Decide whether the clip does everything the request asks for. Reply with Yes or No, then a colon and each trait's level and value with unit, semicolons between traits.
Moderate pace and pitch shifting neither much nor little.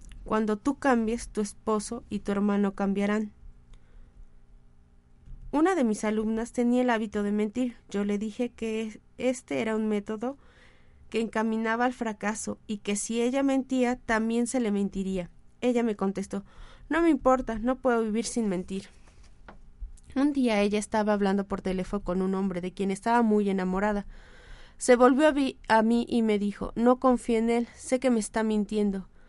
Yes: average, 170 wpm; average, 3.1 semitones